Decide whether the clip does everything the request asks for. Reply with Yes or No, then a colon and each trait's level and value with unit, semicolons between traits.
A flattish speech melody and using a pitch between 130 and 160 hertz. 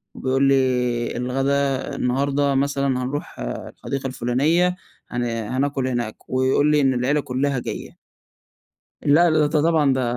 Yes: narrow, 2.1 semitones; low, 135 Hz